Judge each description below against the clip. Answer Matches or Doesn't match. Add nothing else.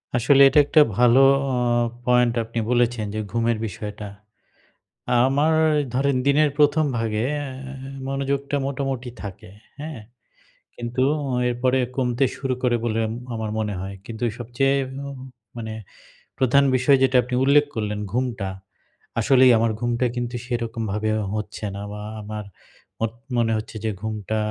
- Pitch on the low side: Matches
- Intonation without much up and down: Doesn't match